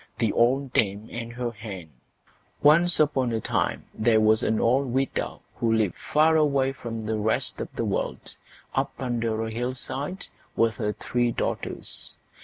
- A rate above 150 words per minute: Yes, average, 160 wpm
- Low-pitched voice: Yes, low, 120 Hz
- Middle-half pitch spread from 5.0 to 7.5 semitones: No, average, 3.3 semitones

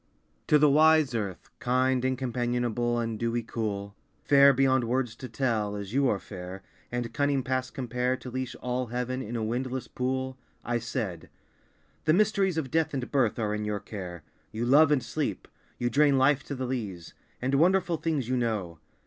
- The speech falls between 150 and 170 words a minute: No, average, 185 wpm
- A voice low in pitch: Yes, low, 125 Hz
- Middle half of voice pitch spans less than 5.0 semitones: Yes, average, 3.0 semitones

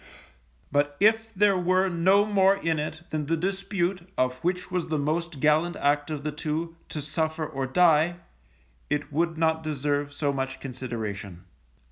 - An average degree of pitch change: Yes, average, 3.7 semitones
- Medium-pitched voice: Yes, medium, 160 Hz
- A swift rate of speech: No, average, 160 wpm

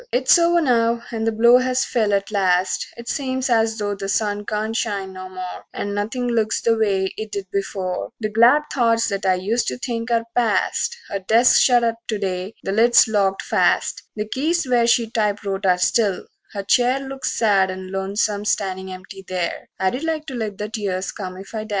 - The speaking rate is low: No, fast, 205 wpm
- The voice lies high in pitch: Yes, high, 215 Hz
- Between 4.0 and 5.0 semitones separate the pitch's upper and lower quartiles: No, average, 3.3 semitones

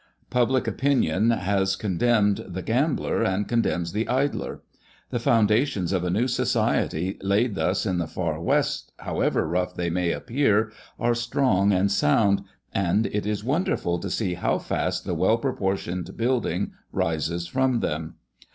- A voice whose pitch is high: No, low, 100 Hz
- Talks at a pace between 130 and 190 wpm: Yes, average, 150 wpm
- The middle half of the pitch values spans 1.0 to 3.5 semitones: No, average, 4.7 semitones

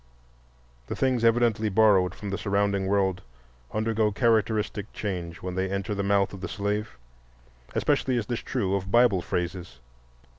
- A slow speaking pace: No, average, 150 wpm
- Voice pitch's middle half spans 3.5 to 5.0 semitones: No, narrow, 2.5 semitones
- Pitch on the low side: Yes, low, 100 Hz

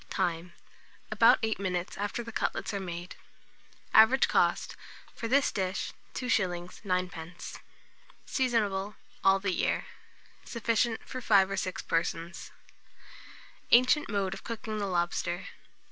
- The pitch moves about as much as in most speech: Yes, average, 3.7 semitones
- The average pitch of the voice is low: No, high, 195 Hz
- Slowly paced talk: Yes, slow, 120 wpm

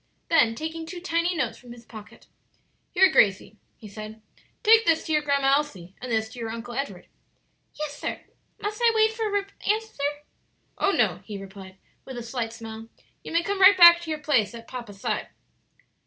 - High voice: Yes, very high, 280 Hz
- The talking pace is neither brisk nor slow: Yes, average, 190 wpm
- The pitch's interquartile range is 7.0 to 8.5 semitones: Yes, wide, 7.3 semitones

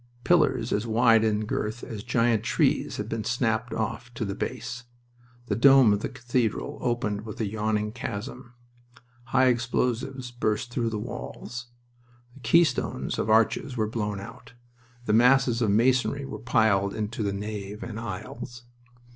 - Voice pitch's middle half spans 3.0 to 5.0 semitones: No, narrow, 2.5 semitones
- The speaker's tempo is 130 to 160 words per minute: Yes, average, 155 wpm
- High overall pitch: No, low, 115 Hz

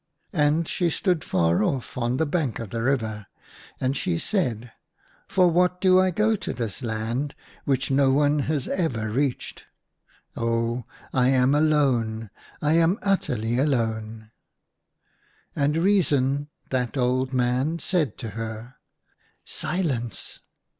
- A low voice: Yes, low, 130 Hz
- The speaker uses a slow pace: No, average, 150 wpm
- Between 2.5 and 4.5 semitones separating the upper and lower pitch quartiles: No, average, 5.1 semitones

